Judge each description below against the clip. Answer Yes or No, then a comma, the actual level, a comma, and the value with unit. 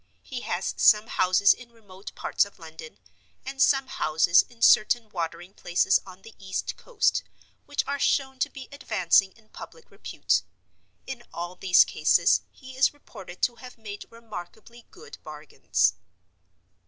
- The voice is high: Yes, high, 215 Hz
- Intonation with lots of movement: Yes, wide, 5.9 semitones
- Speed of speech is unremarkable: Yes, average, 150 wpm